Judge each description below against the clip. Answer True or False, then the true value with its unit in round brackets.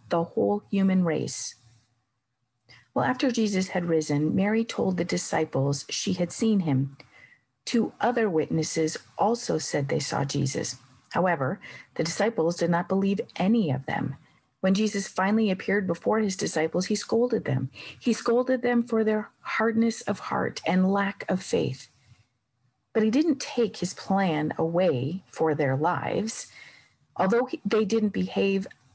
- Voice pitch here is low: False (190 Hz)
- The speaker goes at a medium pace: True (145 wpm)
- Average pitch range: False (5.8 semitones)